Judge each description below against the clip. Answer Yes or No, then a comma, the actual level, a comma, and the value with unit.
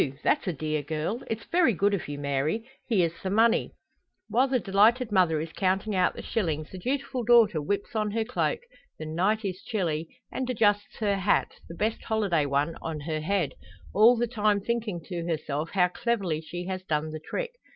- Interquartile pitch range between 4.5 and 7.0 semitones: Yes, wide, 5.6 semitones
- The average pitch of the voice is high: Yes, high, 195 Hz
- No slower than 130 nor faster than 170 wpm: No, average, 195 wpm